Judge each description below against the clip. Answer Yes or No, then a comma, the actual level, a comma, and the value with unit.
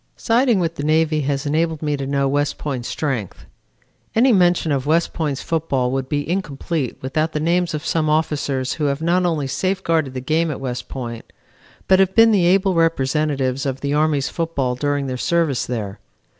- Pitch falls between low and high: Yes, medium, 150 Hz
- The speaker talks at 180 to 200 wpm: Yes, average, 185 wpm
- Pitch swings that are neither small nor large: Yes, average, 3.6 semitones